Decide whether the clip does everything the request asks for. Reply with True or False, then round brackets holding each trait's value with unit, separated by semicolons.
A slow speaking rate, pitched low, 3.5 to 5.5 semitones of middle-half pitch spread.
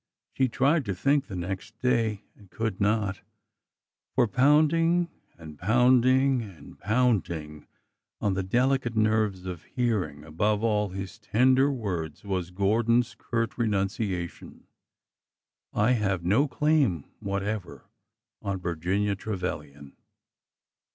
True (115 wpm; 105 Hz; 4.8 semitones)